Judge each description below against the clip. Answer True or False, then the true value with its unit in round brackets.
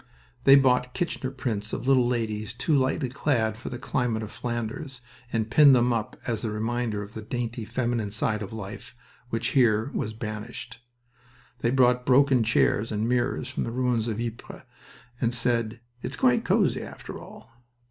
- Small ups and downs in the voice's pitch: True (2.3 semitones)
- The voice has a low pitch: True (120 Hz)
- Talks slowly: False (170 wpm)